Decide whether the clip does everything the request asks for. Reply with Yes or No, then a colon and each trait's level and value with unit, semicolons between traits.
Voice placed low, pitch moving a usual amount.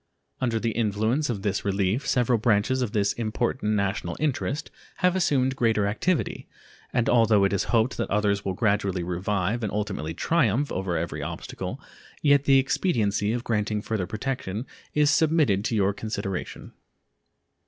Yes: low, 110 Hz; average, 4.2 semitones